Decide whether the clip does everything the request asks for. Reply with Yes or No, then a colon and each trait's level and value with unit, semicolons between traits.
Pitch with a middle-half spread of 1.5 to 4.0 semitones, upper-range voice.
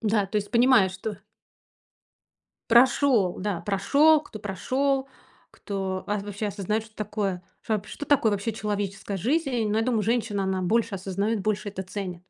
Yes: average, 2.9 semitones; high, 210 Hz